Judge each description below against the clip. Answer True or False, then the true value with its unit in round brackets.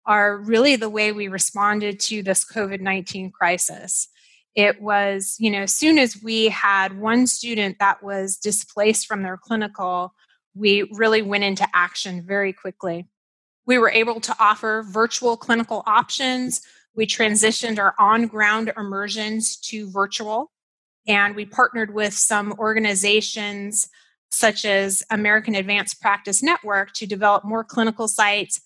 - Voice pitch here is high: True (210 Hz)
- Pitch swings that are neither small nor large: False (1.9 semitones)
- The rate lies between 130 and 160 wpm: True (140 wpm)